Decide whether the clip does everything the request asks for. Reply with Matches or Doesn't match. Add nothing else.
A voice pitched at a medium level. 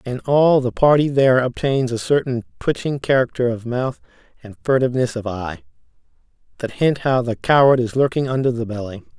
Doesn't match